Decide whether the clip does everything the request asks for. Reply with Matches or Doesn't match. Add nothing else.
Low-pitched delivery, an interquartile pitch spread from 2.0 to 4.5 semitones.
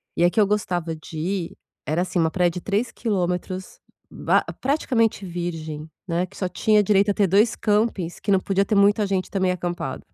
Doesn't match